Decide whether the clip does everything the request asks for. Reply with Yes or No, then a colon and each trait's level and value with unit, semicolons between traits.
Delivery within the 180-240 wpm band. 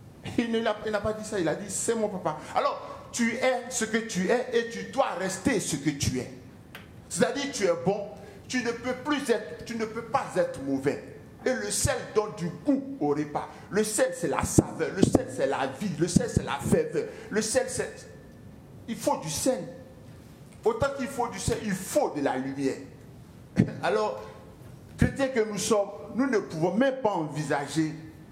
Yes: fast, 205 wpm